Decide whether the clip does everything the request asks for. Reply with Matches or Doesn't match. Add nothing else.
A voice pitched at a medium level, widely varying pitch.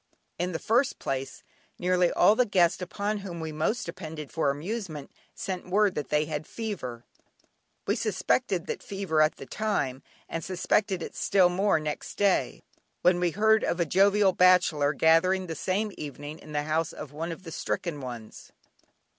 Doesn't match